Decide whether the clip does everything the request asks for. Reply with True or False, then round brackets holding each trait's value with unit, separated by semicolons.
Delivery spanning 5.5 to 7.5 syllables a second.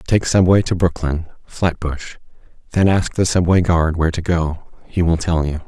False (5.1 syllables/s)